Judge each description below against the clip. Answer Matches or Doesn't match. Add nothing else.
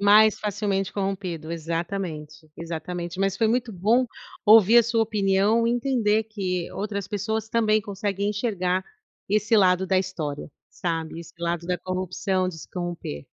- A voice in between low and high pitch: Doesn't match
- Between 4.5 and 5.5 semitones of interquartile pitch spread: Doesn't match